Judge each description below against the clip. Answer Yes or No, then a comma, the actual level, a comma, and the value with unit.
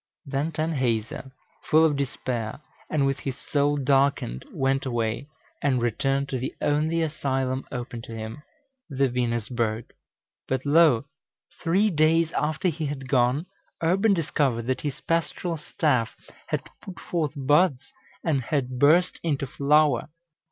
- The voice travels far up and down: No, average, 3.6 semitones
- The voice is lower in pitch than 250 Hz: Yes, medium, 140 Hz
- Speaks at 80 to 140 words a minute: Yes, slow, 135 wpm